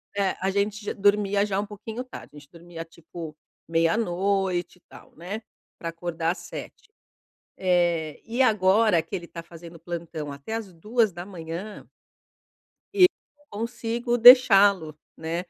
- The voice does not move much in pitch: No, average, 4.2 semitones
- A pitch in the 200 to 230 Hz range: No, medium, 185 Hz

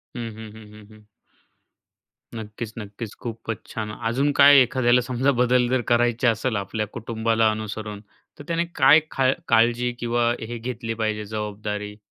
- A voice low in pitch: Yes, low, 115 Hz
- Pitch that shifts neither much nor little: No, narrow, 2.3 semitones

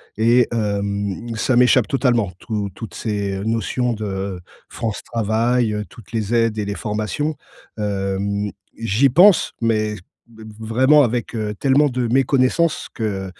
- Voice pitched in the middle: No, low, 110 Hz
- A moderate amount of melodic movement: Yes, average, 3.1 semitones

